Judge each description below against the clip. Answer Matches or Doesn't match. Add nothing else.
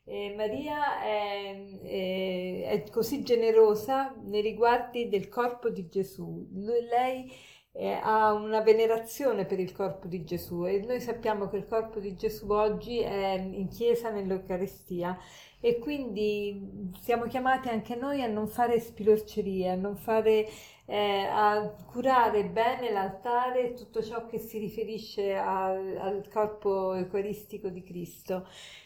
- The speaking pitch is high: Matches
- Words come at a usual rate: Matches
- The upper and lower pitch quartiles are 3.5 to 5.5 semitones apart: Doesn't match